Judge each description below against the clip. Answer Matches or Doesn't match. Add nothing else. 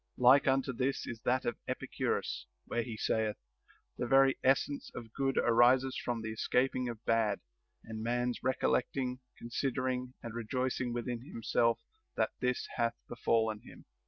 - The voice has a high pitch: Doesn't match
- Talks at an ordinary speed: Matches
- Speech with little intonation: Matches